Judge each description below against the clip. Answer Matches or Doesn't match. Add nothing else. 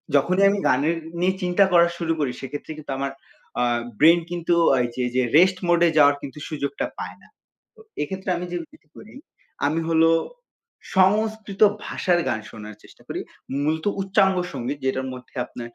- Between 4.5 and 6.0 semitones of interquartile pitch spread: Matches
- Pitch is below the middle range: Doesn't match